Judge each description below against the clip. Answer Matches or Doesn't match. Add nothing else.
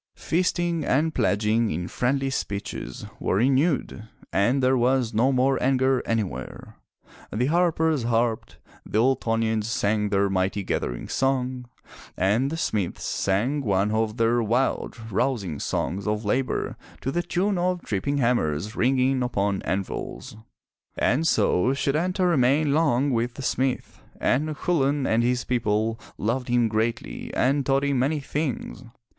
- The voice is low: Matches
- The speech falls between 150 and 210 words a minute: Doesn't match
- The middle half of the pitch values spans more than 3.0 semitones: Matches